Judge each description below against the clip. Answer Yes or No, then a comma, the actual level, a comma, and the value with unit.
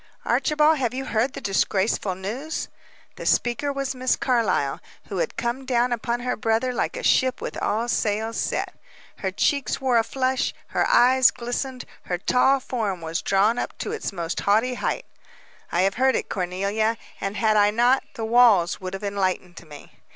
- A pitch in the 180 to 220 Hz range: No, high, 230 Hz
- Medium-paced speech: Yes, average, 180 wpm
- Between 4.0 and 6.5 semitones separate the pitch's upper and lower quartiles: Yes, average, 4.6 semitones